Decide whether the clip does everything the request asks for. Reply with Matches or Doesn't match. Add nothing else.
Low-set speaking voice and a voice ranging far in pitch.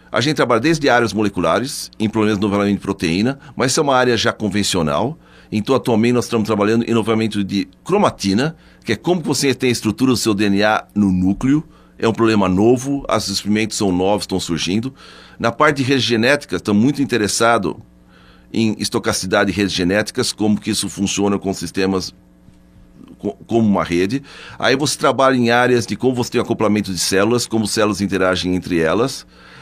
Doesn't match